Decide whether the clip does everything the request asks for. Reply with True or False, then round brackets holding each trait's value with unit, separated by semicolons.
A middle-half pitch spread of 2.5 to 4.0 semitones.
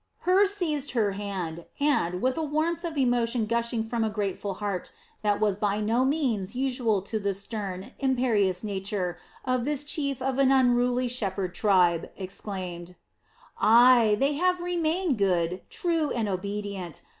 False (5.4 semitones)